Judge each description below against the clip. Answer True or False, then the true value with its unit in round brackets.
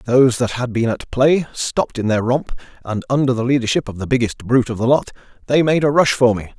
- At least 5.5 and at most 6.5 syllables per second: True (6.0 syllables/s)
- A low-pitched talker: True (125 Hz)